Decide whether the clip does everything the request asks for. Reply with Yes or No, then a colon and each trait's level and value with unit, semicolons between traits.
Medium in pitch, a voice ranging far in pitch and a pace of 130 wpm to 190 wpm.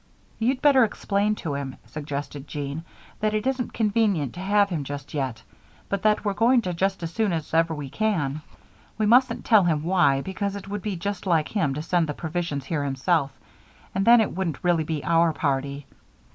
No: medium, 175 Hz; wide, 5.9 semitones; average, 200 wpm